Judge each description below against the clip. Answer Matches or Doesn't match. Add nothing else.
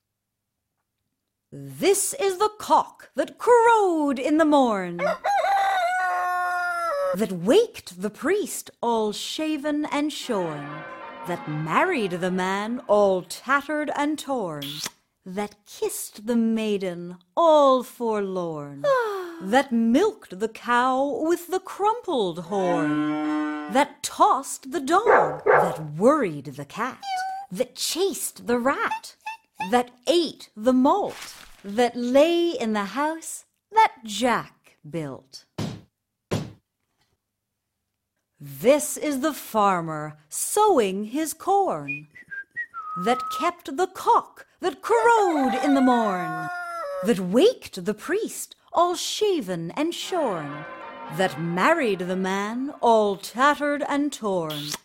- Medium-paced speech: Doesn't match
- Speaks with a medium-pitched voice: Doesn't match